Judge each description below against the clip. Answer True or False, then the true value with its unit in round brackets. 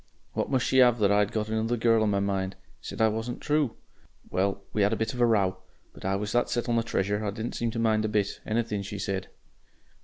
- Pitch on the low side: True (110 Hz)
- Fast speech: True (255 wpm)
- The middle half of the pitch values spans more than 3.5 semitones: False (2.5 semitones)